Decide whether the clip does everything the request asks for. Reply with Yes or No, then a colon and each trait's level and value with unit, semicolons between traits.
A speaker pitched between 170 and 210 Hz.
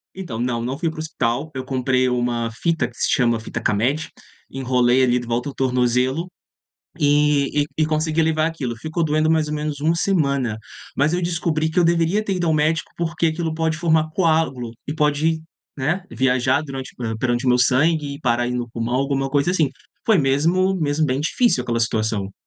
No: medium, 145 Hz